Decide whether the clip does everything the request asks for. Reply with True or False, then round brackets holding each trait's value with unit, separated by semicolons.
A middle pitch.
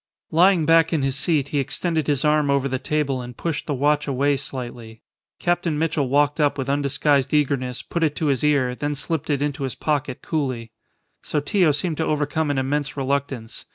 True (145 Hz)